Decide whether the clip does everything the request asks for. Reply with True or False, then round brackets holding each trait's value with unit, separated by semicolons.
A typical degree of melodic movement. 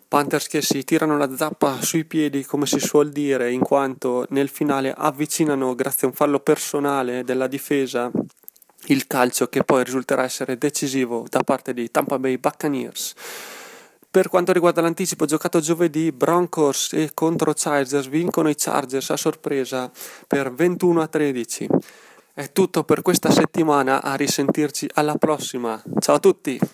True (3.0 semitones)